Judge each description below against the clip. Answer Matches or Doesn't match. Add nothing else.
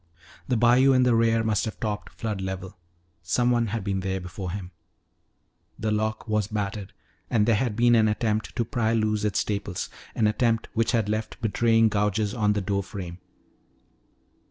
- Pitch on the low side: Matches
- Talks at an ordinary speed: Matches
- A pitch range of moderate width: Doesn't match